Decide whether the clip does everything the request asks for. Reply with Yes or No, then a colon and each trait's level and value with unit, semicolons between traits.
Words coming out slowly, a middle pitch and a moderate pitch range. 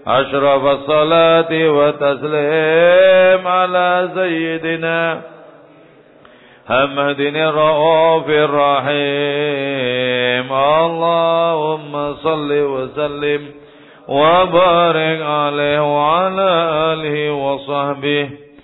No: slow, 50 wpm; medium, 150 Hz; narrow, 2.3 semitones